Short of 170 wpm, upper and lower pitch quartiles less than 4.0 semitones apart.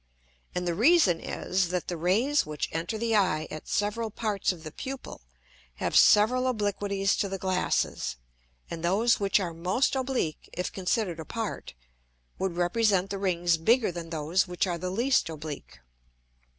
No: average, 160 wpm; average, 4.3 semitones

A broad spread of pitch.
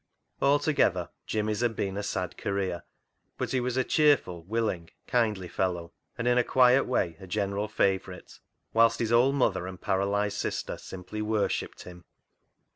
No: average, 4.4 semitones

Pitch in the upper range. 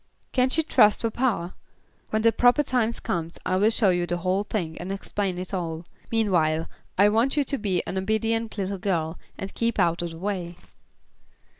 Yes: high, 195 Hz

